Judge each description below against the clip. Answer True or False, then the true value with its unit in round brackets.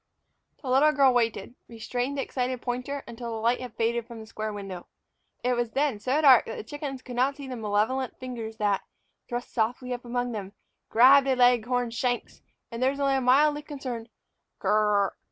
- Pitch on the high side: True (245 Hz)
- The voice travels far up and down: False (2.7 semitones)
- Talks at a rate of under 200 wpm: False (205 wpm)